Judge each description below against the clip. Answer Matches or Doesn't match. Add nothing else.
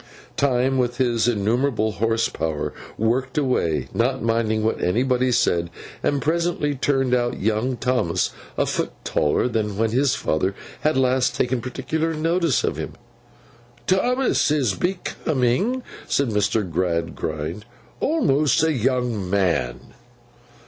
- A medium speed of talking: Doesn't match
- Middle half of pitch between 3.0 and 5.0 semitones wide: Matches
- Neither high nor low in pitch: Doesn't match